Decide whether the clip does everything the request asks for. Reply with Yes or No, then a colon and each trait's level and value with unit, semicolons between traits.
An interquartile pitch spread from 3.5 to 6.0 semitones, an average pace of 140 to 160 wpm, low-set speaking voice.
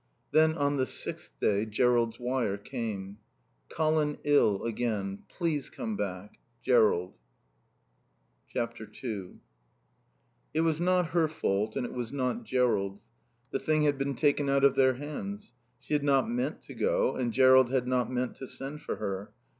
Yes: average, 5.2 semitones; average, 155 wpm; low, 130 Hz